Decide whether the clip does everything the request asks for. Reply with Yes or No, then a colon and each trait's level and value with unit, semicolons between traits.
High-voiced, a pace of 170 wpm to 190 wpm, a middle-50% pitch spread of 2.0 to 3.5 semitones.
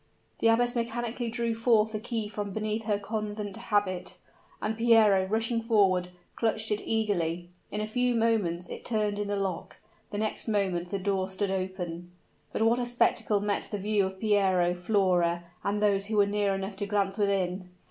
Yes: high, 205 Hz; average, 180 wpm; narrow, 2.6 semitones